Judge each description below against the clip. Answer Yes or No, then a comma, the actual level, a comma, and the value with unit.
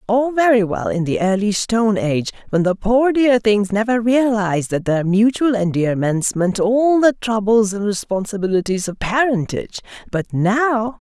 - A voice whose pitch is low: No, high, 210 Hz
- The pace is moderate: Yes, average, 150 wpm